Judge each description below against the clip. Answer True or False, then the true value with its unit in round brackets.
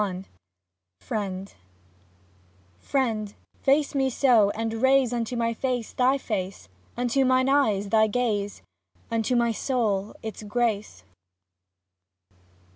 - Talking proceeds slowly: True (110 wpm)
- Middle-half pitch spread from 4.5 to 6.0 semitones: False (3.8 semitones)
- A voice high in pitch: True (230 Hz)